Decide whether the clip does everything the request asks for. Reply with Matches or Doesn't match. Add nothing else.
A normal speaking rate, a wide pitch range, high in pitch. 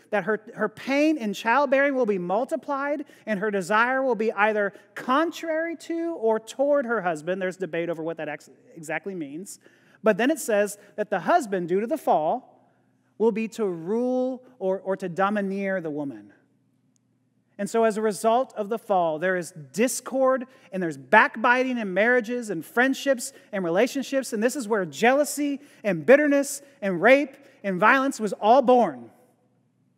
Matches